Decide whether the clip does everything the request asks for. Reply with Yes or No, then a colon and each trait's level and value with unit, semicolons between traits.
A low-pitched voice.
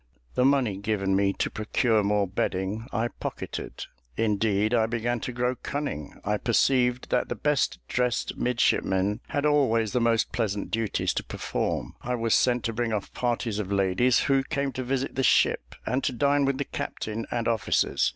Yes: low, 115 Hz